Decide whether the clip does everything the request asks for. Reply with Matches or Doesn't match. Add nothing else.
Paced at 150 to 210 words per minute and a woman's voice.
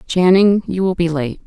Matches